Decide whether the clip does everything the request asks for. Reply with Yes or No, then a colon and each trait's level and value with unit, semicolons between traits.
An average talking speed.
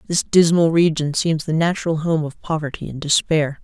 Yes: average, 180 wpm